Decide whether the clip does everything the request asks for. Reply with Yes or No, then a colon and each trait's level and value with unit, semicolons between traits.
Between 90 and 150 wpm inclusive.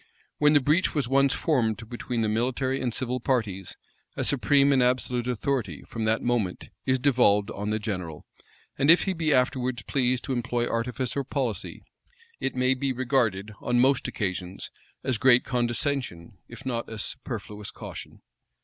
No: average, 165 wpm